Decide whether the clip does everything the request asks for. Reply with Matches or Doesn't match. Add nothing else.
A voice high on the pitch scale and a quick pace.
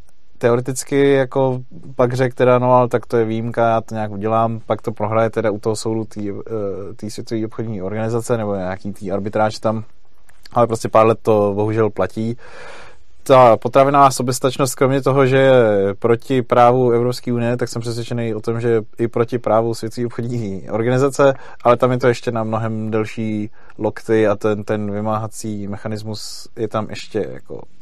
Doesn't match